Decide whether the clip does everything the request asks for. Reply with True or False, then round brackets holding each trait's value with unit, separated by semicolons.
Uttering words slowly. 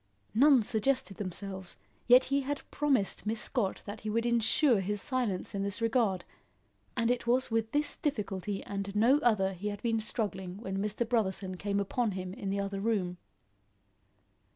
False (170 wpm)